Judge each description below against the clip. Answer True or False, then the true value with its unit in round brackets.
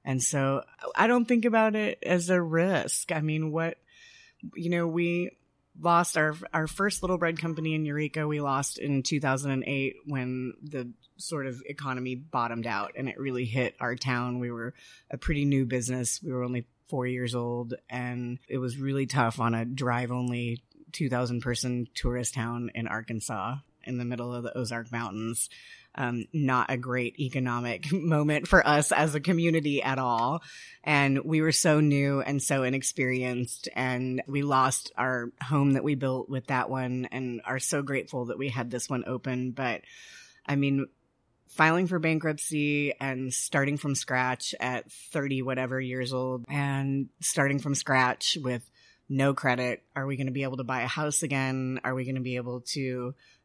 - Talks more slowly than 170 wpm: False (175 wpm)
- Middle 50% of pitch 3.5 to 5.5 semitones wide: False (3.1 semitones)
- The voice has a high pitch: False (135 Hz)